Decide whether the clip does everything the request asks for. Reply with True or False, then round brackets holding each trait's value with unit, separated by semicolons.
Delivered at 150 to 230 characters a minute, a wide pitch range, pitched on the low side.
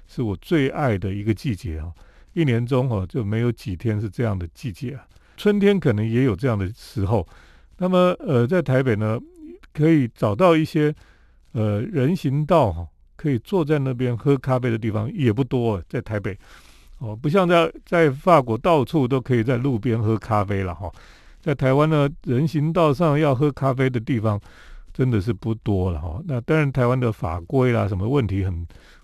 False (265 characters per minute; 6.0 semitones; 125 Hz)